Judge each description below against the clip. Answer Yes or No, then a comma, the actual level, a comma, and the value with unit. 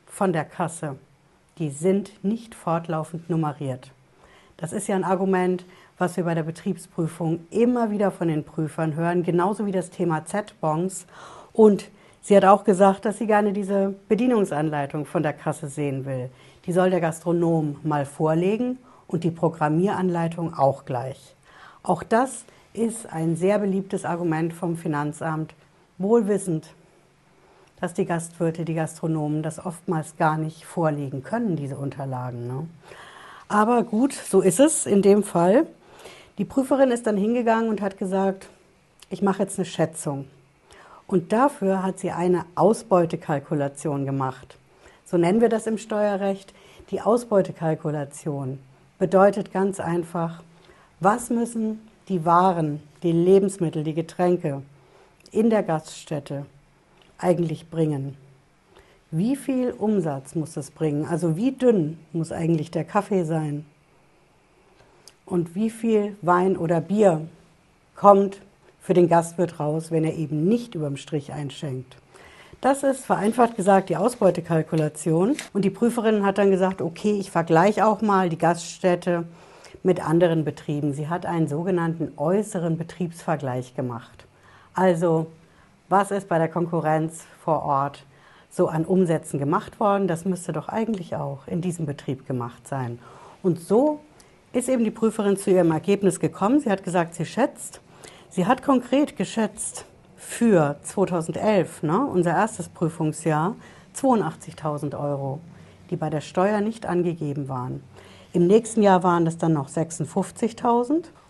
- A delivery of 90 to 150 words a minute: Yes, average, 140 wpm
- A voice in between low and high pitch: Yes, medium, 175 Hz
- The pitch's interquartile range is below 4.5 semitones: Yes, average, 4.0 semitones